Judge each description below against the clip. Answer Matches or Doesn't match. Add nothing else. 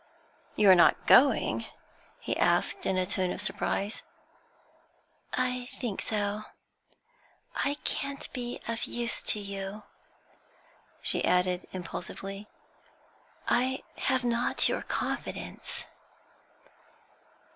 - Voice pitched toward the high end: Matches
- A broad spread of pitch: Doesn't match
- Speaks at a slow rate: Matches